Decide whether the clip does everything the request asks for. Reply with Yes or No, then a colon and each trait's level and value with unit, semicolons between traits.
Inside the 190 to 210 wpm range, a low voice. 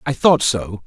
Yes: fast, 205 wpm; low, 120 Hz